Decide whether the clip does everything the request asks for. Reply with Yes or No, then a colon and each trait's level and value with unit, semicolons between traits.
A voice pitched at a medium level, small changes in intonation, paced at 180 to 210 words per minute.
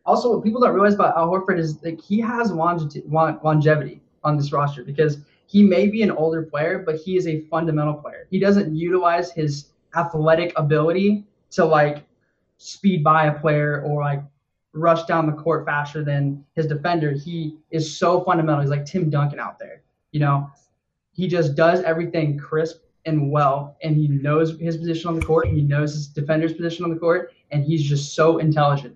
Yes: medium, 160 Hz; narrow, 2.3 semitones; average, 195 wpm